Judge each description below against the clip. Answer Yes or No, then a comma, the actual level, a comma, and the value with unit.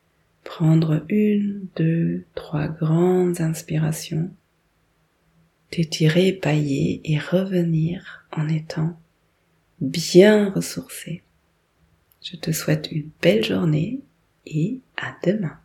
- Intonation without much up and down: Yes, narrow, 2.3 semitones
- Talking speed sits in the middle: No, slow, 90 wpm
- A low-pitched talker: No, medium, 165 Hz